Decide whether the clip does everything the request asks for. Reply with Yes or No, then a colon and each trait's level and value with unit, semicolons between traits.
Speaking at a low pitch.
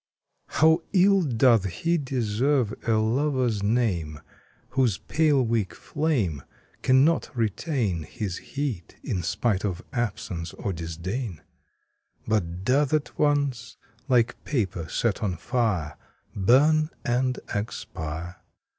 Yes: low, 115 Hz